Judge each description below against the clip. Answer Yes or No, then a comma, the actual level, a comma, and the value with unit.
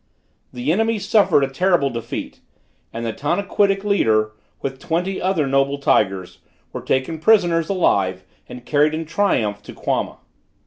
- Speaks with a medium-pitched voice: Yes, medium, 150 Hz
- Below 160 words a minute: Yes, average, 140 wpm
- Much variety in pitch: Yes, wide, 7.5 semitones